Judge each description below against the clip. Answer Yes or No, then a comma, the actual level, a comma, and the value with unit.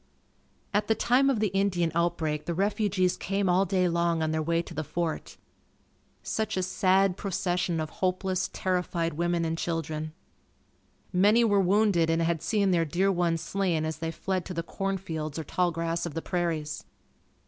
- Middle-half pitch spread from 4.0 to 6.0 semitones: No, average, 2.9 semitones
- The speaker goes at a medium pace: Yes, average, 180 wpm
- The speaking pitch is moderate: Yes, medium, 175 Hz